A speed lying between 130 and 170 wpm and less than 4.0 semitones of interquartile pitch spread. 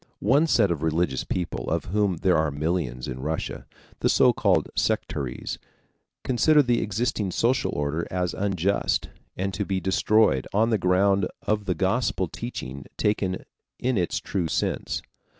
No: average, 150 wpm; average, 4.7 semitones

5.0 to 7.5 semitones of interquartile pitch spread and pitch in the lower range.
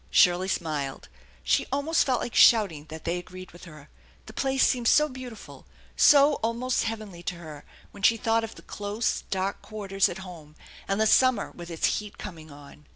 No: average, 5.3 semitones; high, 195 Hz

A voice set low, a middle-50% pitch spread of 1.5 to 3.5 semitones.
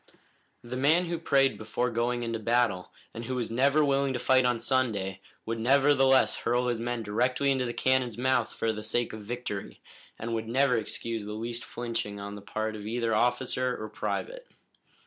Yes: low, 120 Hz; average, 2.8 semitones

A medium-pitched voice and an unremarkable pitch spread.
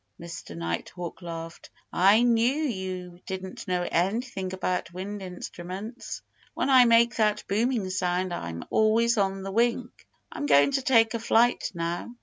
No: high, 195 Hz; average, 4.7 semitones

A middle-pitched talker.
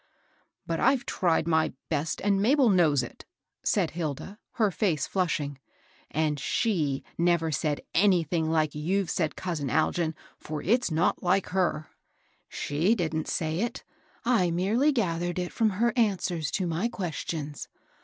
Yes: medium, 170 Hz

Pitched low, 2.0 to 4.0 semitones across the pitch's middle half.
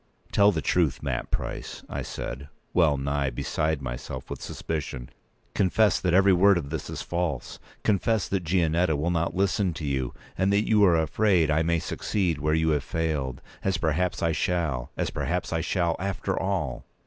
Yes: very low, 85 Hz; average, 3.7 semitones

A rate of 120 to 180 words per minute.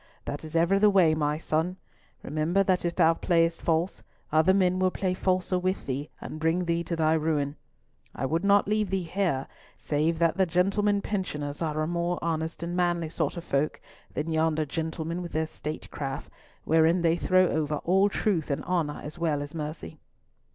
No: average, 190 wpm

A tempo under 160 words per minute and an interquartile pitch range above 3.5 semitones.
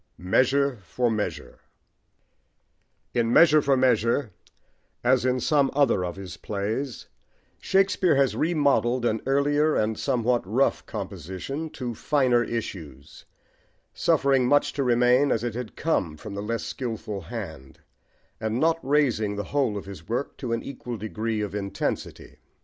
Yes: average, 140 wpm; average, 4.7 semitones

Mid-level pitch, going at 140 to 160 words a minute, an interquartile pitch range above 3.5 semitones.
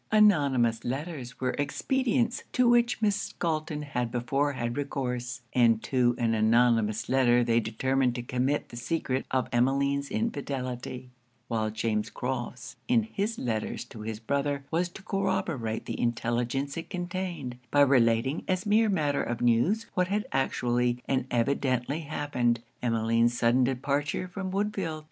No: low, 130 Hz; average, 145 wpm; average, 5.3 semitones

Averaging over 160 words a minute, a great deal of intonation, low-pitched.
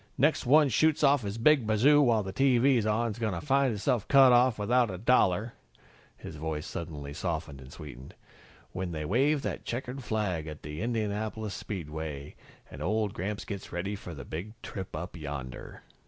Yes: average, 180 wpm; wide, 7.1 semitones; low, 105 Hz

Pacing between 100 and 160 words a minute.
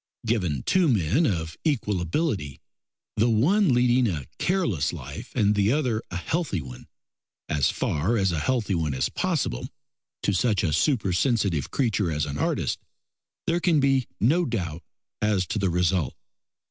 Yes: average, 155 wpm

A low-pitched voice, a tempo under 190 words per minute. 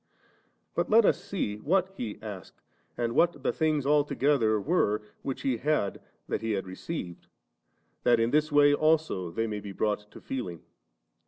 Yes: low, 125 Hz; average, 165 wpm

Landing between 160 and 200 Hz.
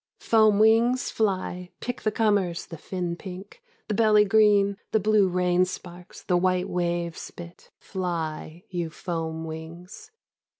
Yes: medium, 185 Hz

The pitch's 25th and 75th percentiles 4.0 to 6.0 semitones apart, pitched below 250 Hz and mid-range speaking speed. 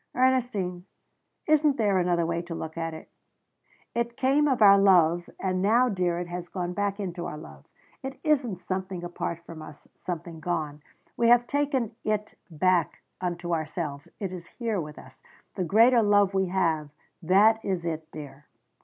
Yes: average, 4.4 semitones; medium, 185 Hz; average, 170 wpm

